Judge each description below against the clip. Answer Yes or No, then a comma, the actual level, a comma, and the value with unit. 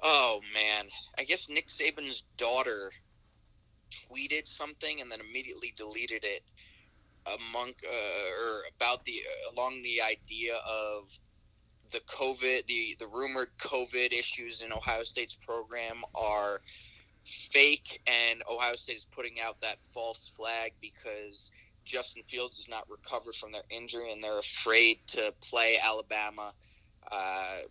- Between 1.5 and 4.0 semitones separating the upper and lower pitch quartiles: Yes, average, 3.0 semitones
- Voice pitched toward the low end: Yes, low, 115 Hz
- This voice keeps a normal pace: No, slow, 130 wpm